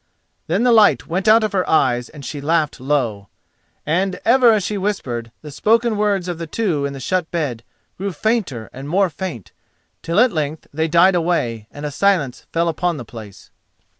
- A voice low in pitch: No, medium, 165 Hz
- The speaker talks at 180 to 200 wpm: Yes, average, 195 wpm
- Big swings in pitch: Yes, wide, 5.8 semitones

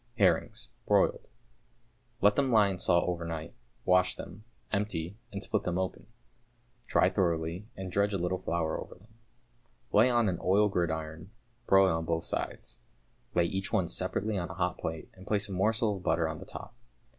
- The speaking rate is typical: Yes, average, 175 wpm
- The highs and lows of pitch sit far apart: No, average, 3.4 semitones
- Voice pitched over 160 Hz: No, very low, 95 Hz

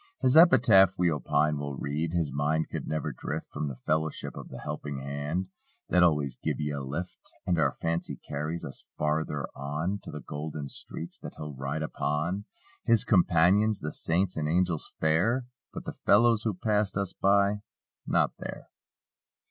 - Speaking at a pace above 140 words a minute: Yes, average, 170 wpm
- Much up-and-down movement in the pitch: No, average, 4.5 semitones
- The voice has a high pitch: No, very low, 80 Hz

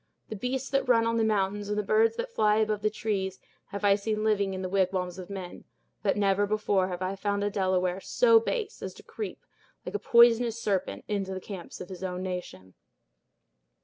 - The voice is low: No, high, 205 Hz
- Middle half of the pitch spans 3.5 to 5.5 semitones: No, average, 2.9 semitones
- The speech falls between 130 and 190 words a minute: No, fast, 205 wpm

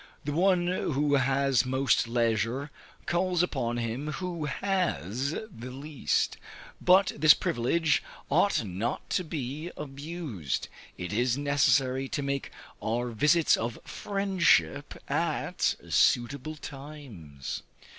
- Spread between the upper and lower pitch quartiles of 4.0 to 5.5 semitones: Yes, average, 4.6 semitones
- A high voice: No, medium, 140 Hz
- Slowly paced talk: Yes, slow, 110 wpm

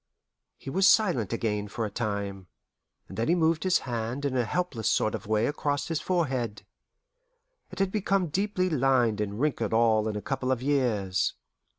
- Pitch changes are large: Yes, wide, 6.7 semitones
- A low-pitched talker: Yes, low, 125 Hz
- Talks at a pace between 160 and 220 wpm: Yes, average, 180 wpm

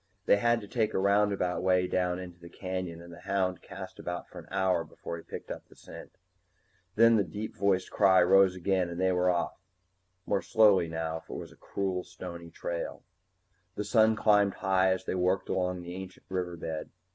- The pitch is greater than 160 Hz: No, very low, 95 Hz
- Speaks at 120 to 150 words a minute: No, fast, 205 wpm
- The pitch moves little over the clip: Yes, narrow, 2.0 semitones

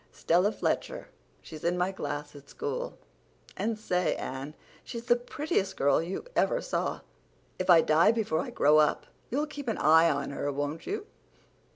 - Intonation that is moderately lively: No, wide, 7.4 semitones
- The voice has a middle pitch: Yes, medium, 180 Hz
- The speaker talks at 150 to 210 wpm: Yes, average, 170 wpm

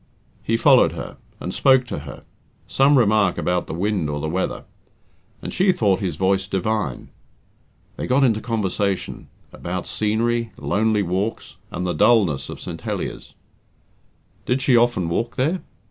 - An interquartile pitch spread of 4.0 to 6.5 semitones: Yes, average, 4.6 semitones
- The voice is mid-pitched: No, low, 105 Hz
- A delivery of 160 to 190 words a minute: No, average, 150 wpm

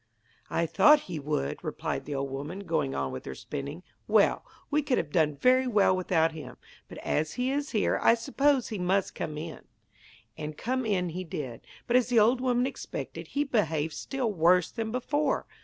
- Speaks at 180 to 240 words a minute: Yes, average, 190 wpm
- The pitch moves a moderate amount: No, wide, 8.5 semitones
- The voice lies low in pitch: No, medium, 185 Hz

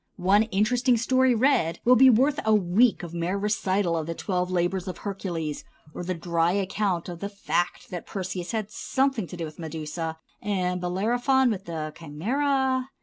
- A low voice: No, high, 190 Hz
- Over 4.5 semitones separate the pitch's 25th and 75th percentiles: Yes, average, 5.0 semitones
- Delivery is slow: No, average, 175 wpm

